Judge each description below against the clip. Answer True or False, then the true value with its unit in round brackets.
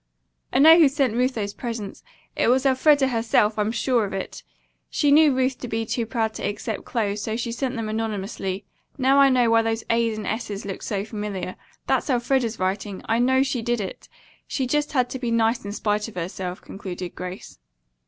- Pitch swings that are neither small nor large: True (3.7 semitones)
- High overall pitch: True (225 Hz)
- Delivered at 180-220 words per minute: True (200 wpm)